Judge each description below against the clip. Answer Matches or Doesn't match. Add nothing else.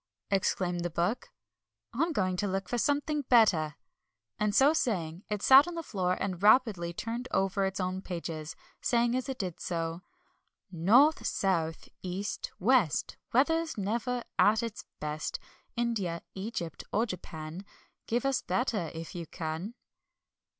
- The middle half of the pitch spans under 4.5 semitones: Doesn't match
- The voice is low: Doesn't match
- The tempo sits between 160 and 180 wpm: Doesn't match